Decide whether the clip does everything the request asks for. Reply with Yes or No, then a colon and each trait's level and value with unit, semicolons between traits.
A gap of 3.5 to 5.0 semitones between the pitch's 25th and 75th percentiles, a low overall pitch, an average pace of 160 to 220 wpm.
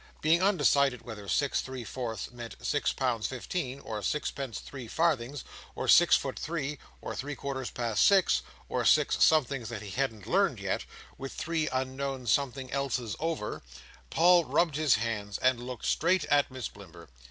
Yes: average, 3.9 semitones; low, 130 Hz; average, 165 wpm